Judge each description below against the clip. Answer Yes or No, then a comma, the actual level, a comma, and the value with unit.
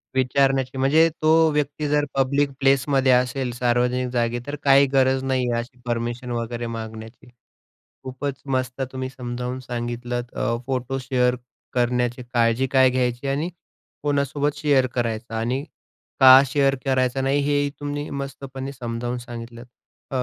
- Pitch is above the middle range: No, low, 130 Hz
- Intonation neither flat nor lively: No, narrow, 2.1 semitones